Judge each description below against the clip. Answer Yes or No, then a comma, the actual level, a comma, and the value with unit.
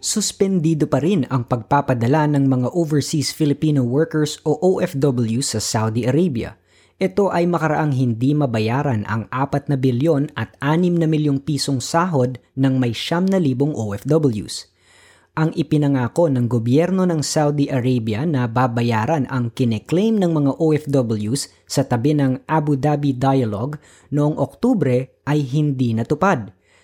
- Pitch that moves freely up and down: No, average, 3.8 semitones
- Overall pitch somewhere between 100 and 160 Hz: Yes, medium, 140 Hz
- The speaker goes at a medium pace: Yes, average, 135 wpm